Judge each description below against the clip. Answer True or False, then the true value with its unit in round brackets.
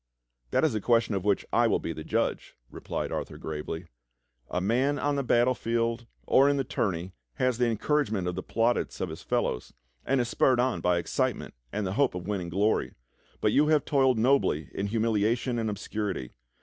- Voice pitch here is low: True (115 Hz)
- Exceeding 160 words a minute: True (200 wpm)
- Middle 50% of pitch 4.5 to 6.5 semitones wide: True (5.2 semitones)